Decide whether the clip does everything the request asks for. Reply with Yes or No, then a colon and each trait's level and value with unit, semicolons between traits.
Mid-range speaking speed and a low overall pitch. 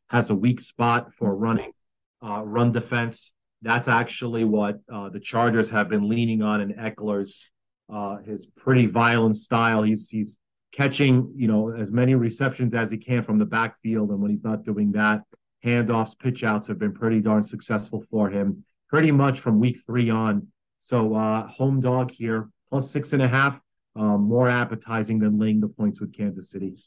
Yes: average, 180 wpm; low, 110 Hz